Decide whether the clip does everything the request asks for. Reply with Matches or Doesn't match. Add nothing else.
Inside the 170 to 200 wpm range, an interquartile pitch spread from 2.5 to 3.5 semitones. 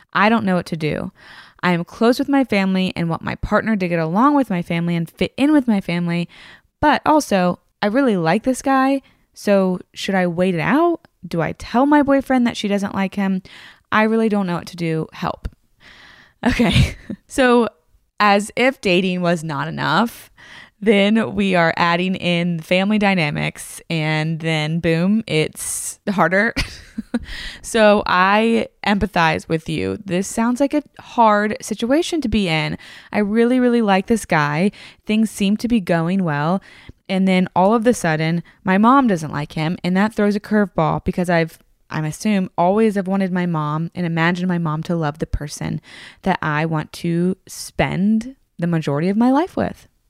Doesn't match